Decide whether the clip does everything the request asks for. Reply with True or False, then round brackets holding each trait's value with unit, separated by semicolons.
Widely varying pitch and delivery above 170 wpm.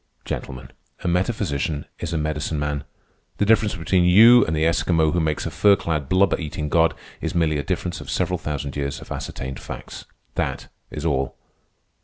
False (3.5 semitones; 180 wpm)